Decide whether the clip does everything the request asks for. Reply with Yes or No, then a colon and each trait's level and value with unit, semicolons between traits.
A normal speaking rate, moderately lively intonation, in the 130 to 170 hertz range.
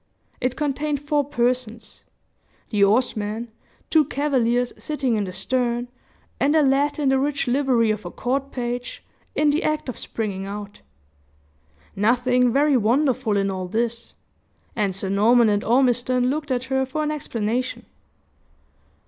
No: average, 145 wpm; average, 3.8 semitones; very high, 250 Hz